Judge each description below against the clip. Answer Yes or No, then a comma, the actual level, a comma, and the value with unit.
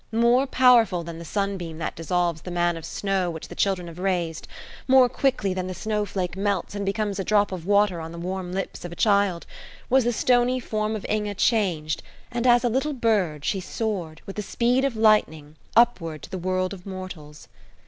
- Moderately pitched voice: No, high, 195 Hz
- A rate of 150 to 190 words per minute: No, average, 200 wpm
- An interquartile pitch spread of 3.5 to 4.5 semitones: Yes, average, 4.1 semitones